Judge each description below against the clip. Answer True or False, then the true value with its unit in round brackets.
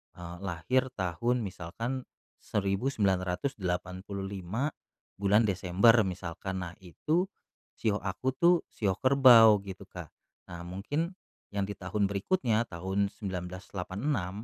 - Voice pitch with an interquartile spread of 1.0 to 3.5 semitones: False (4.2 semitones)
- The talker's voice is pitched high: False (100 Hz)